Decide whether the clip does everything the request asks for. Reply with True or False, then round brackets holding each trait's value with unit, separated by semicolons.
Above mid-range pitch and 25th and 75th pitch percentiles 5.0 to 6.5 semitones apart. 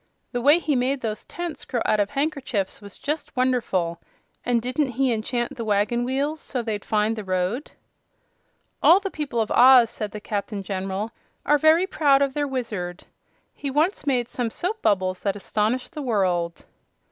True (245 Hz; 5.3 semitones)